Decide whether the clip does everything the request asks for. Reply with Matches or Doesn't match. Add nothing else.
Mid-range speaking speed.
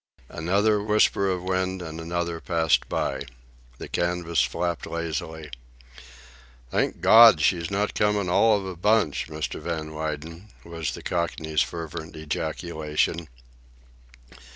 Doesn't match